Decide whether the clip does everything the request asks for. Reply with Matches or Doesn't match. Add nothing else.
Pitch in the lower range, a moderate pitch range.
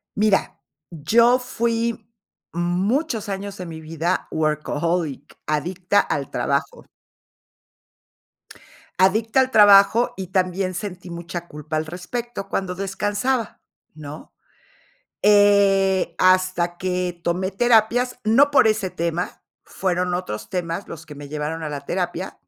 Doesn't match